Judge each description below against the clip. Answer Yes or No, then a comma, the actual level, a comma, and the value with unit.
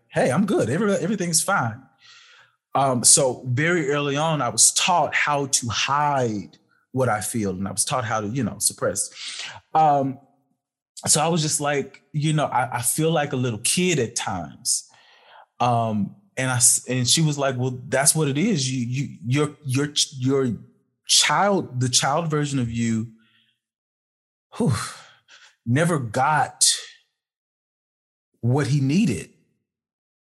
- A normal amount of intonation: Yes, average, 4.2 semitones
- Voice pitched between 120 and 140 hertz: Yes, low, 135 Hz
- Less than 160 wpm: Yes, average, 150 wpm